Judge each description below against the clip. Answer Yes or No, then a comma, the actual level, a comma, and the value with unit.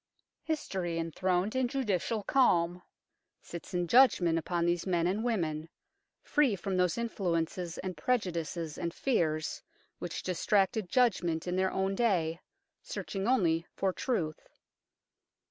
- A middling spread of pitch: Yes, average, 4.4 semitones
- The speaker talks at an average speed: No, slow, 125 wpm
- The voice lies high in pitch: No, medium, 180 Hz